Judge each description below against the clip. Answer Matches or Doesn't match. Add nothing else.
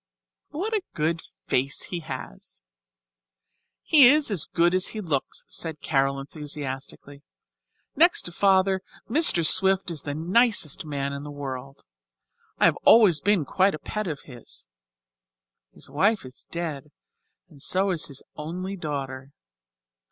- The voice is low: Doesn't match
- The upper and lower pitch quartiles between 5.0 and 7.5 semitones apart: Matches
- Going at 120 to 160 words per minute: Matches